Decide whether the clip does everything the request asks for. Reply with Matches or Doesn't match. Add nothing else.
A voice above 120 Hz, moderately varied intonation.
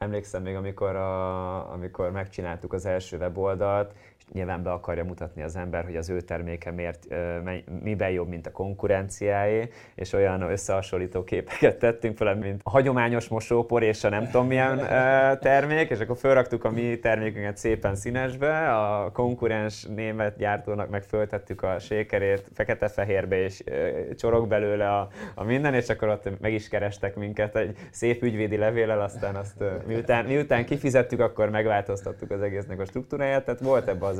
Doesn't match